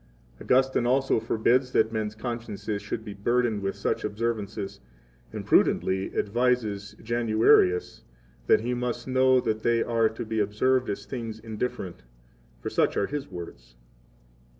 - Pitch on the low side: Yes, low, 115 Hz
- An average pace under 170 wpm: Yes, average, 145 wpm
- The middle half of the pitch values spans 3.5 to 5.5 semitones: No, average, 2.8 semitones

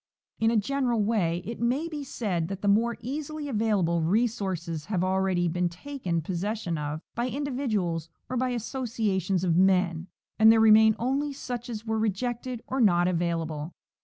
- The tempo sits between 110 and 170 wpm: Yes, average, 165 wpm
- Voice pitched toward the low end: No, high, 215 Hz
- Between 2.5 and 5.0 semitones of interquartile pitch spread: No, wide, 5.5 semitones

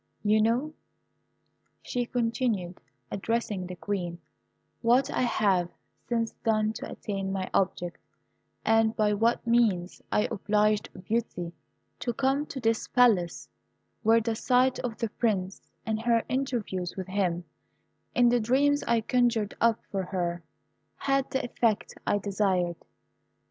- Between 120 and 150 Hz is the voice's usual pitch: No, high, 220 Hz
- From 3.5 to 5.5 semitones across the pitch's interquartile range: Yes, average, 3.9 semitones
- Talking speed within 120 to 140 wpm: Yes, slow, 135 wpm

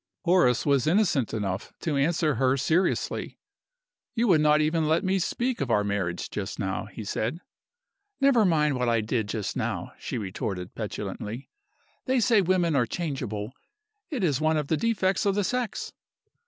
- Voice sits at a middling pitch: Yes, medium, 150 Hz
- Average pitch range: No, wide, 8.7 semitones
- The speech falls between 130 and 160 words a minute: No, average, 170 wpm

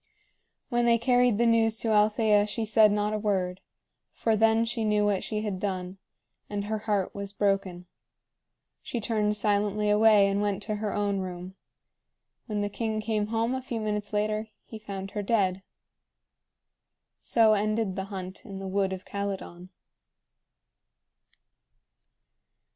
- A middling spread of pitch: No, narrow, 1.8 semitones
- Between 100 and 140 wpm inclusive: No, average, 150 wpm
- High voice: Yes, high, 210 Hz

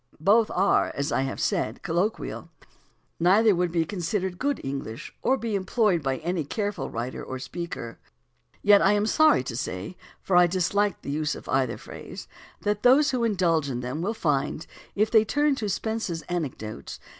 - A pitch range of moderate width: No, wide, 6.5 semitones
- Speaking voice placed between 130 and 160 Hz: No, medium, 180 Hz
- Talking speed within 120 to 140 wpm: No, average, 180 wpm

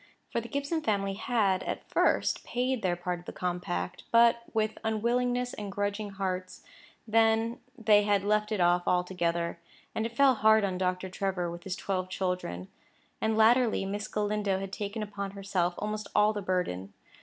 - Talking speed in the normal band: Yes, average, 170 wpm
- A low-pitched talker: No, high, 205 Hz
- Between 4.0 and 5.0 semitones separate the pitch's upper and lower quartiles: No, average, 3.3 semitones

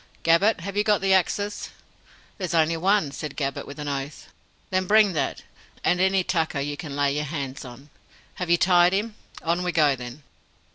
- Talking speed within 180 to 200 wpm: Yes, average, 190 wpm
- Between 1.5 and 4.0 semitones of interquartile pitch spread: No, average, 4.8 semitones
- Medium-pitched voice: Yes, medium, 165 Hz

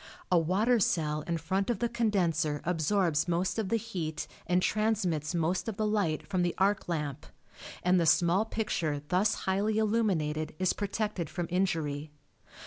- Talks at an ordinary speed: Yes, average, 160 wpm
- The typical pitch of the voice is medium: Yes, medium, 180 Hz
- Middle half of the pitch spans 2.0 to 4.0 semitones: No, average, 4.5 semitones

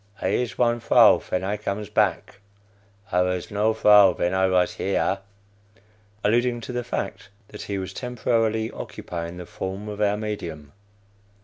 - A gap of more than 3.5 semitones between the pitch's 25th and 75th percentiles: No, average, 2.9 semitones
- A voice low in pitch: Yes, low, 105 Hz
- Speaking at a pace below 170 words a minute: Yes, average, 155 wpm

